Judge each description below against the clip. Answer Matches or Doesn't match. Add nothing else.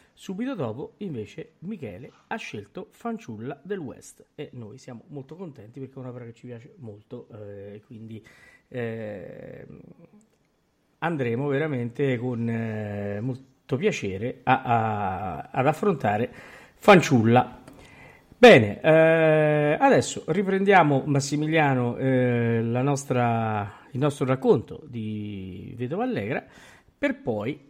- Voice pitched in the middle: Doesn't match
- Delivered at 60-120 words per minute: Matches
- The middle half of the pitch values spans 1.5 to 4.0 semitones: Doesn't match